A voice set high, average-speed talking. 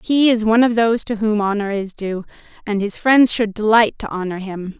No: high, 215 Hz; fast, 225 wpm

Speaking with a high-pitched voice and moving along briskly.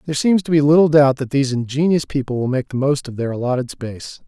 No: medium, 140 Hz; fast, 255 wpm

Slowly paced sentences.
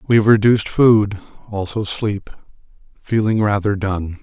Yes: slow, 130 wpm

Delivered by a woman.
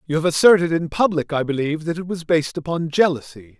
No: male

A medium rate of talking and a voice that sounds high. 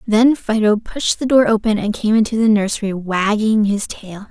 Yes: average, 195 wpm; high, 215 Hz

